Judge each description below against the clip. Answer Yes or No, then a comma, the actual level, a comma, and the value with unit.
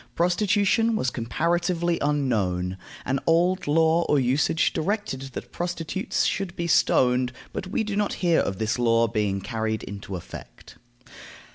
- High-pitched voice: No, medium, 155 Hz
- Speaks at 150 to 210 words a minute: No, average, 140 wpm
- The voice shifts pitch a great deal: Yes, wide, 7.5 semitones